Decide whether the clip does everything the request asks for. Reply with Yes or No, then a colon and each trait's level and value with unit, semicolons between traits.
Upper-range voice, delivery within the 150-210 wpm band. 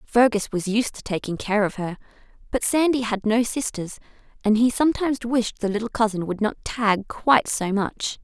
Yes: high, 220 Hz; average, 190 wpm